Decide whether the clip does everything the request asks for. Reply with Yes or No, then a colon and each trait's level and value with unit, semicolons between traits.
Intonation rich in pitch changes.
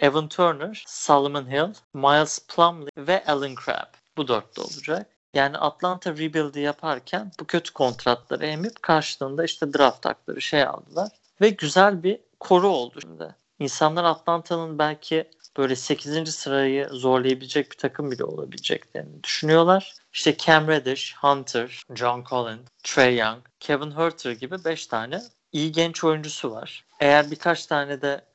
No: average, 3.2 semitones